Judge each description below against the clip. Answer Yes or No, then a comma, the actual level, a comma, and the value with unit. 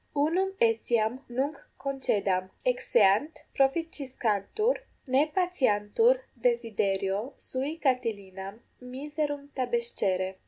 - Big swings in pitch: Yes, wide, 5.9 semitones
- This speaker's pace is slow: Yes, slow, 75 wpm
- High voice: Yes, very high, 255 Hz